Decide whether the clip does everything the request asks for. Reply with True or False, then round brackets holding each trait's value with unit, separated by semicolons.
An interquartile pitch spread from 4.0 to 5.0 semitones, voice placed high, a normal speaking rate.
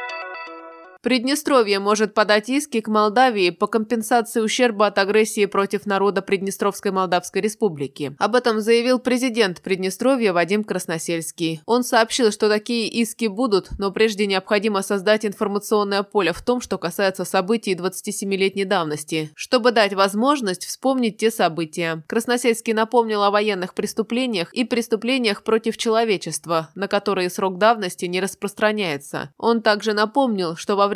False (3.0 semitones; 210 Hz; 135 wpm)